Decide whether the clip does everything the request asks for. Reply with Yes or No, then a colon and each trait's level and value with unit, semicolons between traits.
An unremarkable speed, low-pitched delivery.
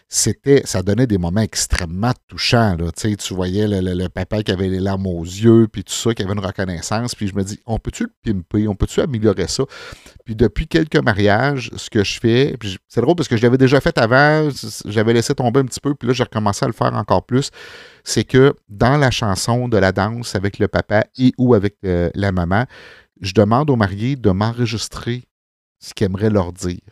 No: fast, 225 wpm; low, 110 Hz